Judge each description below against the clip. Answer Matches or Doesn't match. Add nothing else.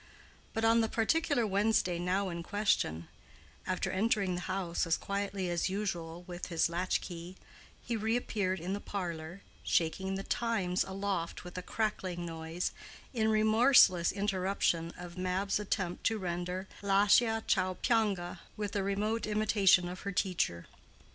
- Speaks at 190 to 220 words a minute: Doesn't match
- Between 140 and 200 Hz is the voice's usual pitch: Matches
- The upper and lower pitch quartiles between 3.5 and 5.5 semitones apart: Doesn't match